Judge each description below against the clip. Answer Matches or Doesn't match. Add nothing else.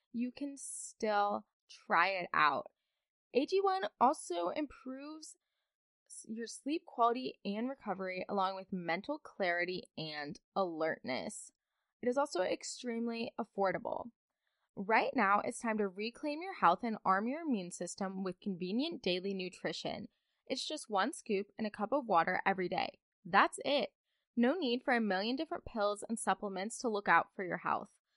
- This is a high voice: Matches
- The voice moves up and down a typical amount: Doesn't match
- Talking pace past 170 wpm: Doesn't match